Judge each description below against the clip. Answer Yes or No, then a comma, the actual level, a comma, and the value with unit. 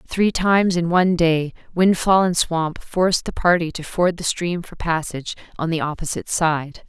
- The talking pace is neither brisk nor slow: Yes, average, 185 wpm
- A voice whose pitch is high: No, medium, 170 Hz